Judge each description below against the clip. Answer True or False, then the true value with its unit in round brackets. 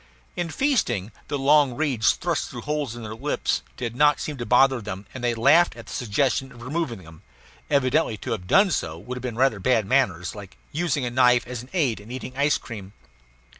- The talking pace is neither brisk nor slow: False (210 wpm)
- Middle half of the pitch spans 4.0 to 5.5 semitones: True (4.4 semitones)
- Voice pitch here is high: False (125 Hz)